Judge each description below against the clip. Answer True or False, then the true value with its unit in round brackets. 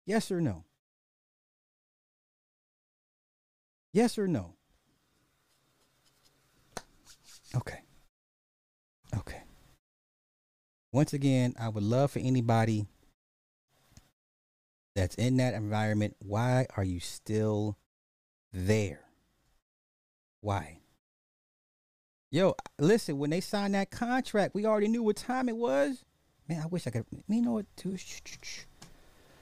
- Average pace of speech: False (105 wpm)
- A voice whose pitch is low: True (120 Hz)